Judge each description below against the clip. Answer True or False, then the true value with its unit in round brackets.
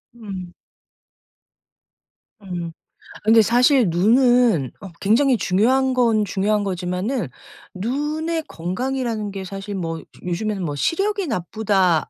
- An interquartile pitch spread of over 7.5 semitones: False (5.3 semitones)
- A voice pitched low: False (210 Hz)